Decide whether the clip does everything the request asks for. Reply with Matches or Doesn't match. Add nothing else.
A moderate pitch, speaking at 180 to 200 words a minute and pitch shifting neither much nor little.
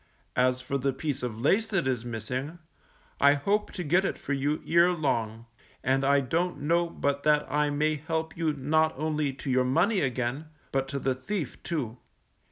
Matches